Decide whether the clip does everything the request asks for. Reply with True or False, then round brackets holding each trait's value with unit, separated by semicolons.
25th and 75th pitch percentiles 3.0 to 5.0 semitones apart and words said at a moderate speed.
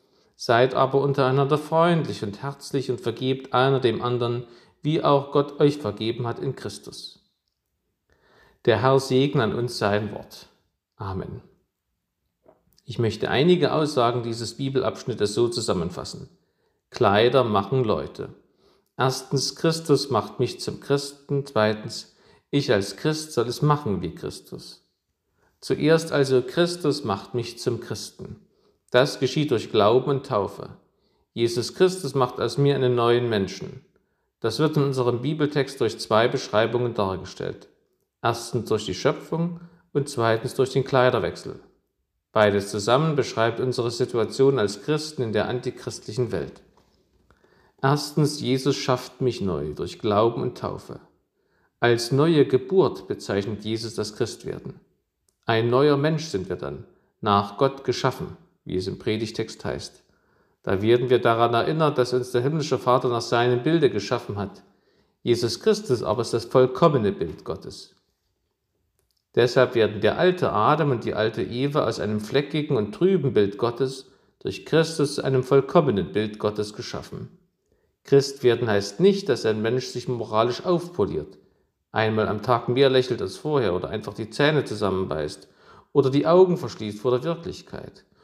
True (4.0 semitones; 140 wpm)